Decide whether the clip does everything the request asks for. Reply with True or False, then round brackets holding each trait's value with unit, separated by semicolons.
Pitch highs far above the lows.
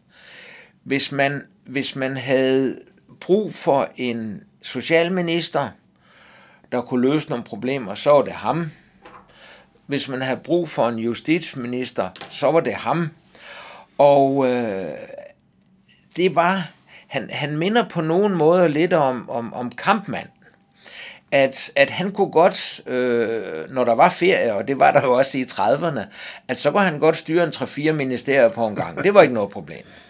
False (4.9 semitones)